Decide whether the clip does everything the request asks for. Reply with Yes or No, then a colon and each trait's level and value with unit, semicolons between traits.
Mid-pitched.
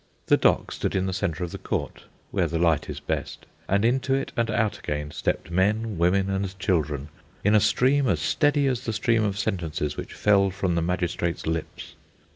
No: very low, 95 Hz